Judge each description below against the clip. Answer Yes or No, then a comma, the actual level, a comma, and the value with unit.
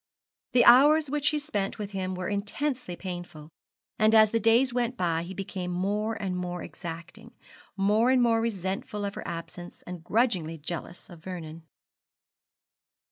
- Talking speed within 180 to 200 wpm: No, average, 155 wpm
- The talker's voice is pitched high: Yes, high, 195 Hz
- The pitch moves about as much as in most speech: Yes, average, 4.6 semitones